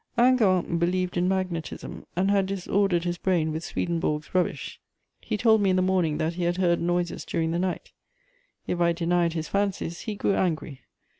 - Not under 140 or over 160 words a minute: No, average, 180 wpm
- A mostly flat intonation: Yes, narrow, 2.0 semitones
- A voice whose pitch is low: No, medium, 175 Hz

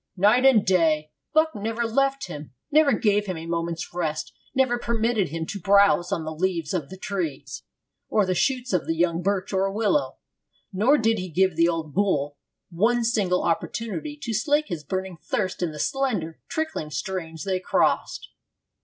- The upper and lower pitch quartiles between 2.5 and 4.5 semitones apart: No, wide, 5.4 semitones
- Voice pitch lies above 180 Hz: Yes, high, 190 Hz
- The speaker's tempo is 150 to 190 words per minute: Yes, average, 175 wpm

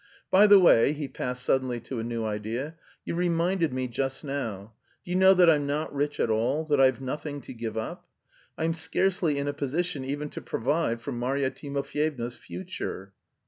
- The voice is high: No, medium, 140 Hz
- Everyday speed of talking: Yes, average, 185 wpm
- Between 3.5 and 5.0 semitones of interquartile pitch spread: Yes, average, 4.7 semitones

